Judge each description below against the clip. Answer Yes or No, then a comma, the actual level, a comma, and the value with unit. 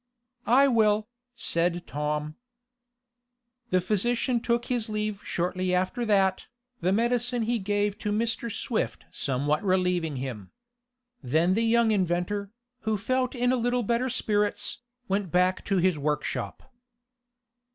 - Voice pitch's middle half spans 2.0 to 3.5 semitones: No, average, 4.6 semitones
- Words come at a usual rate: No, slow, 130 wpm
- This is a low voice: No, high, 205 Hz